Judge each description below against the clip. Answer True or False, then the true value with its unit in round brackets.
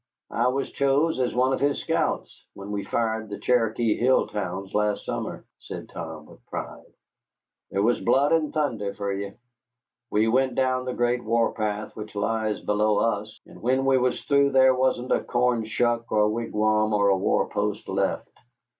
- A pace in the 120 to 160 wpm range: False (180 wpm)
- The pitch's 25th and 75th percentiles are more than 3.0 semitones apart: True (3.5 semitones)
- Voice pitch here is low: True (115 Hz)